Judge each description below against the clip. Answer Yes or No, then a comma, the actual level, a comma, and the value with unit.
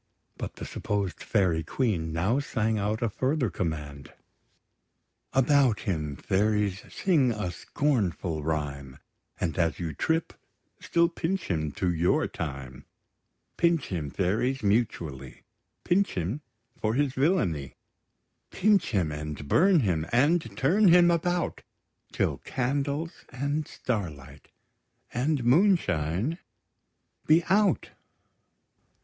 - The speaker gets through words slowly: Yes, slow, 110 wpm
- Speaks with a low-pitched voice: Yes, low, 110 Hz